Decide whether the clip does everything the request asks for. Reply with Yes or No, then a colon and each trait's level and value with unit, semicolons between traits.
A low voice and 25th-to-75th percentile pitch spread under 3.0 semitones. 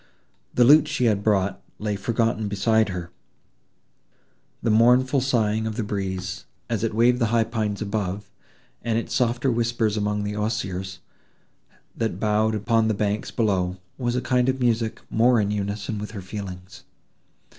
Yes: low, 110 Hz; narrow, 2.5 semitones